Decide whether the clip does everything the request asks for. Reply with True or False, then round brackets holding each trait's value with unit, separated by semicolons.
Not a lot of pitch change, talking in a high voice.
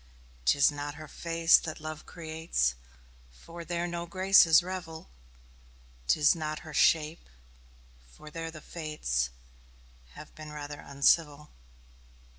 False (2.1 semitones; 155 Hz)